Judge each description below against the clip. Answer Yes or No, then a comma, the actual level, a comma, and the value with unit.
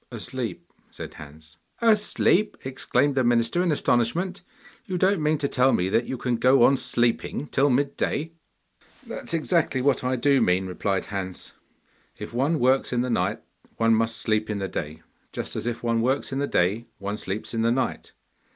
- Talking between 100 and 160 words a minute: No, average, 190 wpm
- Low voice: Yes, low, 125 Hz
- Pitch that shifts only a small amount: No, average, 4.6 semitones